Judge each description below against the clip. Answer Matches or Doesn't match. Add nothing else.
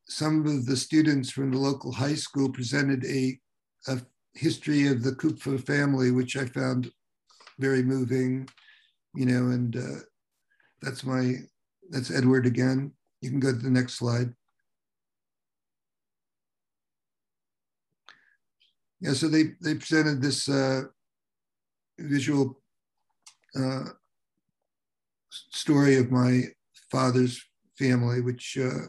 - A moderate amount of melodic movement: Doesn't match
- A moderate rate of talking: Doesn't match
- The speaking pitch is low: Matches